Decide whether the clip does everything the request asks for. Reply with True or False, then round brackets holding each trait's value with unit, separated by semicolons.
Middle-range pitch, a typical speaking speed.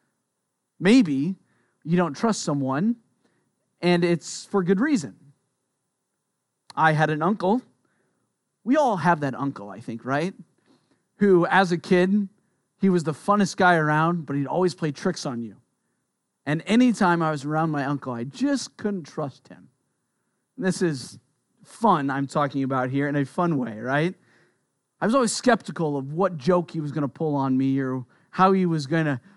True (165 Hz; 170 wpm)